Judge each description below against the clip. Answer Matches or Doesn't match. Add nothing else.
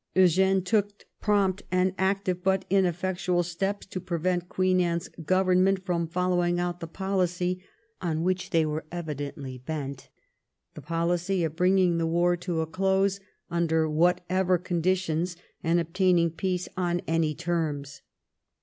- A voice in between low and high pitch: Matches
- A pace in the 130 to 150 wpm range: Matches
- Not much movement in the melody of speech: Matches